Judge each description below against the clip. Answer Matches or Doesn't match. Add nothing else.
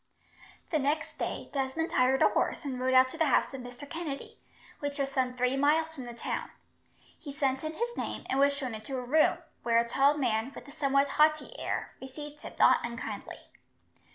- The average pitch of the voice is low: Doesn't match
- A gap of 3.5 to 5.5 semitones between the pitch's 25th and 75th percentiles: Doesn't match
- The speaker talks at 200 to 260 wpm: Matches